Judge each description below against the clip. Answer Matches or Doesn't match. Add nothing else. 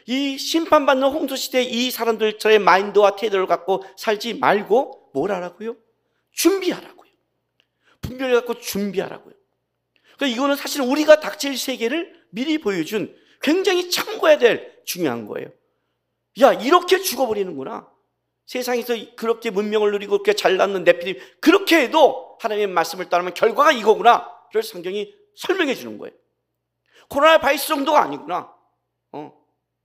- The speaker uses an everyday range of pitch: Doesn't match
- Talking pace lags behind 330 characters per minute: Doesn't match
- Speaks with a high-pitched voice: Matches